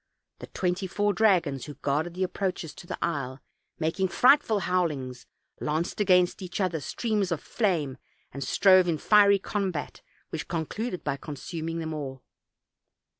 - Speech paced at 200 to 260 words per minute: No, average, 145 wpm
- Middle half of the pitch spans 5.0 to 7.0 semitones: No, average, 4.5 semitones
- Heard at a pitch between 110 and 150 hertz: No, medium, 175 Hz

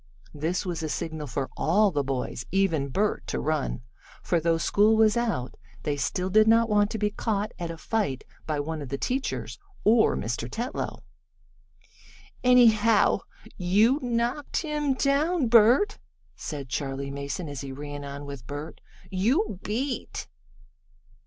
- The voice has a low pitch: No, medium, 185 Hz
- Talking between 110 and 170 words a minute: Yes, average, 150 wpm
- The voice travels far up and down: Yes, wide, 8.0 semitones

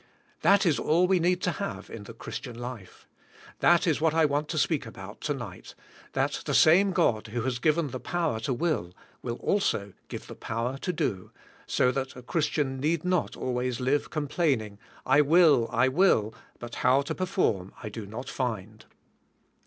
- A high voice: No, low, 135 Hz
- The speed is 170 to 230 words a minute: Yes, average, 185 wpm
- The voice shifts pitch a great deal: Yes, wide, 5.9 semitones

